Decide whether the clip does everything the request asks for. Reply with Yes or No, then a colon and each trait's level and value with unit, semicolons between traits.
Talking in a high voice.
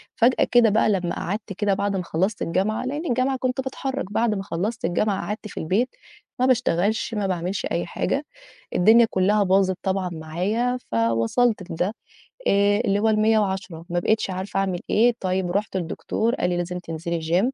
Yes: high, 195 Hz